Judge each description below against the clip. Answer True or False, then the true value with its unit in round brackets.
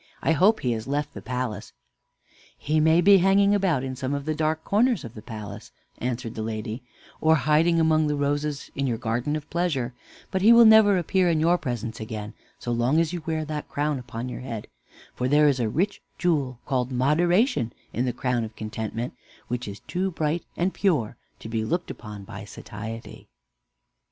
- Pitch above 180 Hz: False (140 Hz)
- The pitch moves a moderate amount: False (5.9 semitones)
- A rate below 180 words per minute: False (190 wpm)